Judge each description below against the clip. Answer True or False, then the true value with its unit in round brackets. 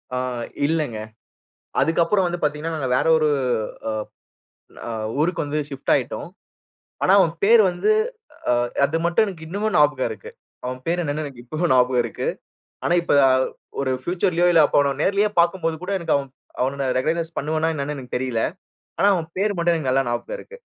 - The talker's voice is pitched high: False (160 Hz)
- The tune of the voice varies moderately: True (4.0 semitones)